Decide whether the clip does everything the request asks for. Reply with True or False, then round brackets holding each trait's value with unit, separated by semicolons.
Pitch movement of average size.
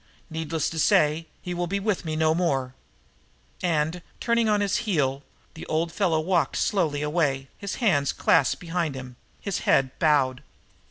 True (3.7 semitones)